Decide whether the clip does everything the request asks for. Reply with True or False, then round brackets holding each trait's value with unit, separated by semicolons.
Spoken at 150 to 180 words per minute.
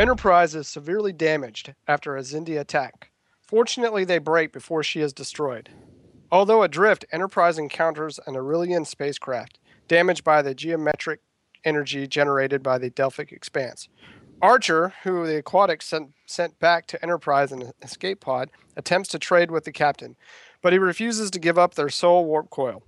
True (160 wpm)